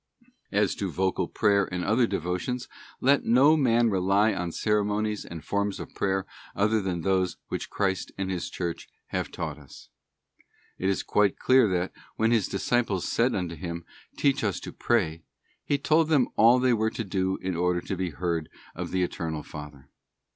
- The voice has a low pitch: Yes, low, 100 Hz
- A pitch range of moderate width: Yes, average, 4.0 semitones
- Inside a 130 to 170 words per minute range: No, average, 185 wpm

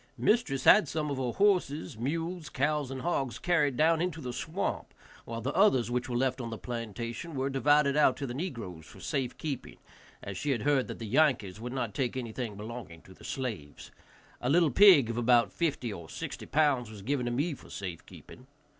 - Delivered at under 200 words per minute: No, fast, 205 wpm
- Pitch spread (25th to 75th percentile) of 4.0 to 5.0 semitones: Yes, average, 4.3 semitones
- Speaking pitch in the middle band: No, low, 130 Hz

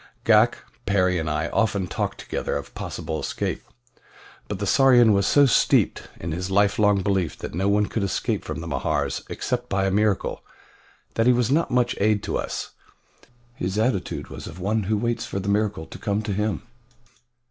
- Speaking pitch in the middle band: No, low, 100 Hz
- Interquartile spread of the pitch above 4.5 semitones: No, average, 2.7 semitones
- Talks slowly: No, average, 185 wpm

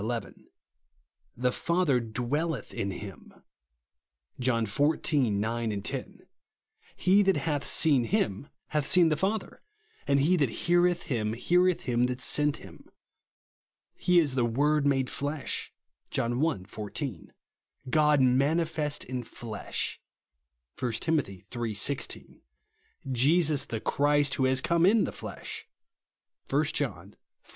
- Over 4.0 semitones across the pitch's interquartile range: Yes, average, 5.2 semitones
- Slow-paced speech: Yes, slow, 130 wpm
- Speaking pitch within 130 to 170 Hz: Yes, medium, 140 Hz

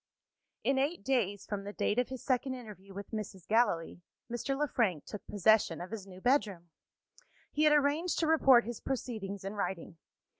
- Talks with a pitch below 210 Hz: No, high, 220 Hz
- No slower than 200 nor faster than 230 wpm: No, average, 180 wpm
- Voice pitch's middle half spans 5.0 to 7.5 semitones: Yes, wide, 5.4 semitones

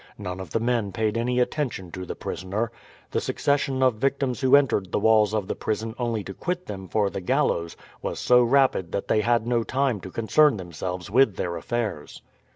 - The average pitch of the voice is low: Yes, low, 110 Hz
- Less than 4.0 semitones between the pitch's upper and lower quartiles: No, average, 4.7 semitones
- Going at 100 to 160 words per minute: No, average, 200 wpm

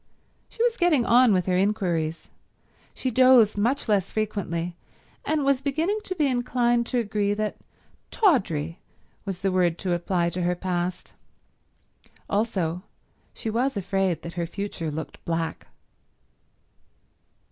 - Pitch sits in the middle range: No, high, 200 Hz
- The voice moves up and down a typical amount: No, wide, 6.0 semitones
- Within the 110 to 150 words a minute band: Yes, slow, 135 wpm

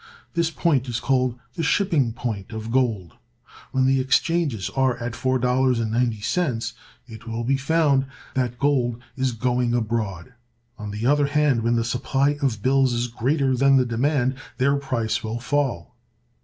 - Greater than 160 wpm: No, average, 155 wpm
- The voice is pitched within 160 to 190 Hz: No, low, 125 Hz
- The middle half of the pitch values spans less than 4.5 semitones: Yes, average, 2.8 semitones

